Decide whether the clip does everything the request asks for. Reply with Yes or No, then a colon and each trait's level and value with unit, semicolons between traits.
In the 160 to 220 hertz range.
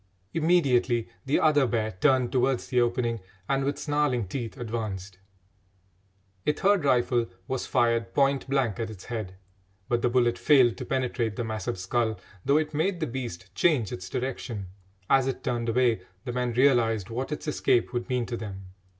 No: low, 120 Hz